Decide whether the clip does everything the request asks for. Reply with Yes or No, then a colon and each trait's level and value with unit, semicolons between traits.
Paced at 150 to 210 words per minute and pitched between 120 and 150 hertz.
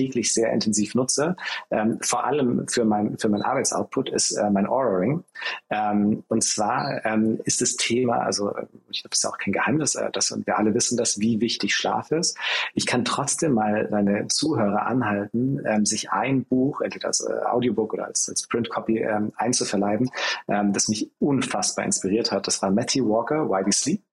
No: average, 185 wpm; low, 110 Hz